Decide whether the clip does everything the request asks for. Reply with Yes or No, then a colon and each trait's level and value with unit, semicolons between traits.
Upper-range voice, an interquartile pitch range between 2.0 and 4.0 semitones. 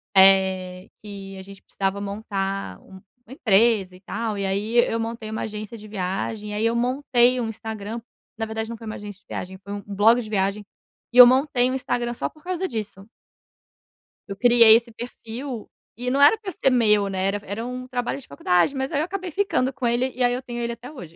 Yes: high, 225 Hz; average, 3.7 semitones